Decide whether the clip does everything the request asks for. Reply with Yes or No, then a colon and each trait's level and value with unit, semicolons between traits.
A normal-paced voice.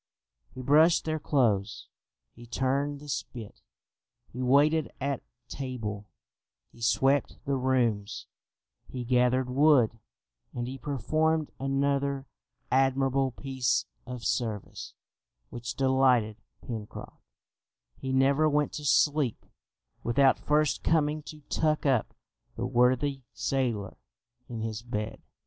No: slow, 110 wpm